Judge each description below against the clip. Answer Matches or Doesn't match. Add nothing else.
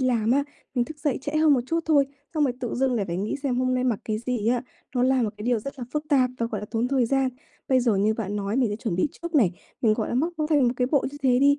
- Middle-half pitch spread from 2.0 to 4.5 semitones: Matches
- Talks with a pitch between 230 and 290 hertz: Matches